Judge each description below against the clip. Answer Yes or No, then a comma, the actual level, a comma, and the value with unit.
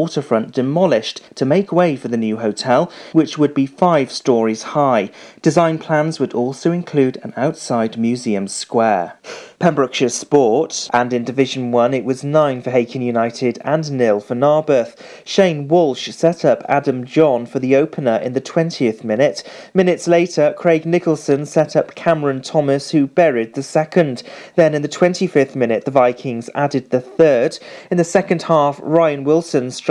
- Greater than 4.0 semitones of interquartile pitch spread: Yes, average, 4.5 semitones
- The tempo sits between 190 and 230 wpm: No, average, 165 wpm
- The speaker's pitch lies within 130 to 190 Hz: Yes, medium, 140 Hz